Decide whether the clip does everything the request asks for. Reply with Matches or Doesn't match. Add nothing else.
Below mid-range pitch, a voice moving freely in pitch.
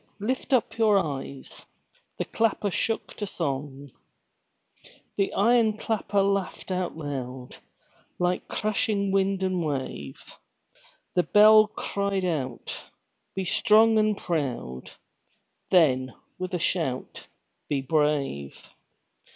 Doesn't match